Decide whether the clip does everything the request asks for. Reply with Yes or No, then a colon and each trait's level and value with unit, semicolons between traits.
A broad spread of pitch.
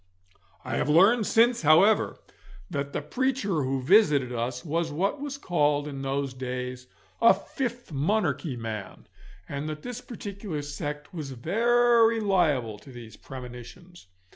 Yes: wide, 8.0 semitones